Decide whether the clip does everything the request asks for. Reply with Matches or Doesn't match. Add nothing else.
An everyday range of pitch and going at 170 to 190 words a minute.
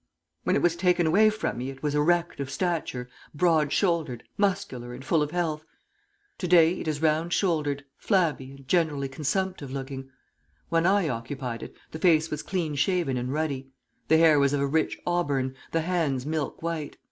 Matches